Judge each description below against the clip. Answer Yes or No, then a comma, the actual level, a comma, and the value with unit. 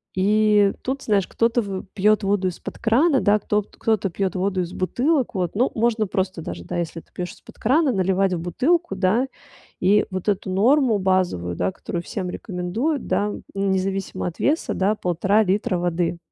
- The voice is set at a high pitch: Yes, high, 195 Hz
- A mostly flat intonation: No, average, 3.2 semitones